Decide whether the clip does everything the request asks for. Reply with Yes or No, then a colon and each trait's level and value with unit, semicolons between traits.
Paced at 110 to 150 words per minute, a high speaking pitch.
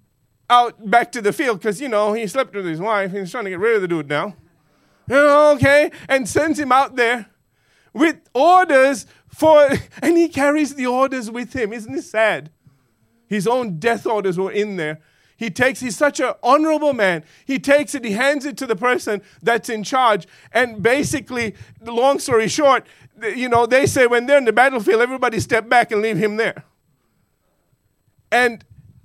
No: average, 185 wpm; high, 235 Hz